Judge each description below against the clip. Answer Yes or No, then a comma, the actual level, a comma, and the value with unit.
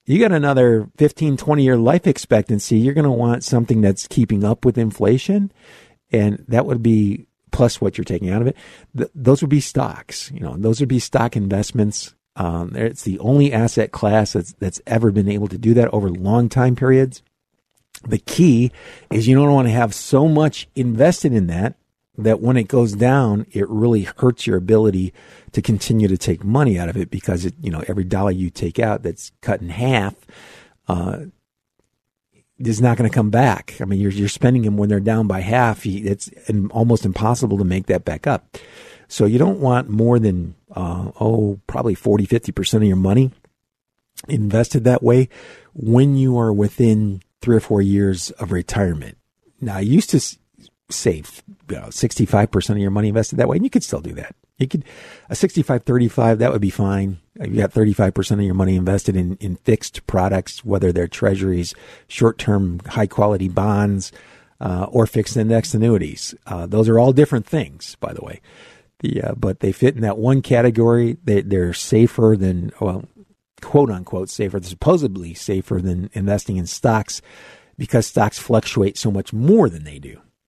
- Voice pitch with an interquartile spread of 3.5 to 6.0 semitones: Yes, average, 4.0 semitones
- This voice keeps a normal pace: Yes, average, 185 wpm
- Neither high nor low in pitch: No, low, 110 Hz